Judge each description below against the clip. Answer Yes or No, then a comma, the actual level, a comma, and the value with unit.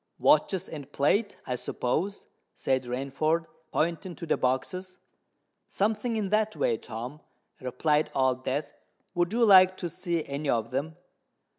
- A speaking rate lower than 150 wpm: Yes, average, 140 wpm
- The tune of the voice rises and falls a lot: Yes, wide, 6.1 semitones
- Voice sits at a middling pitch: Yes, medium, 155 Hz